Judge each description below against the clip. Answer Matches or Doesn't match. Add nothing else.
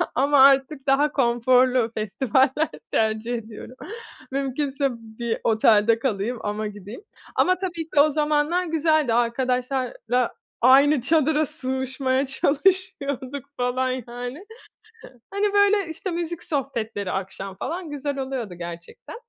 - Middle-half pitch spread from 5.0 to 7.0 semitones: Doesn't match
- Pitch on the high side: Matches